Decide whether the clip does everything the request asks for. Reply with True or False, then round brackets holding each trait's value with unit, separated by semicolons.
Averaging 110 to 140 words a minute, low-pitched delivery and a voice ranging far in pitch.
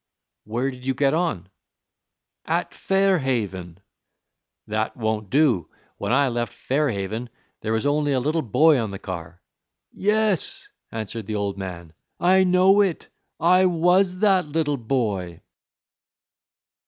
True (135 wpm; 130 Hz; 8.0 semitones)